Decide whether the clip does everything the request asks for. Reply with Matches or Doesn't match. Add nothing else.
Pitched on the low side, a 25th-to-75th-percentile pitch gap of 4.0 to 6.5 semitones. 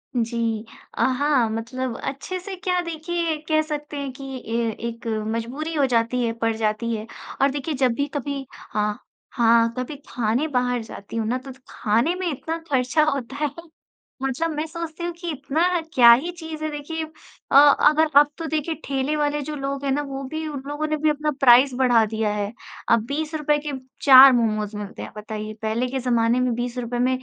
Doesn't match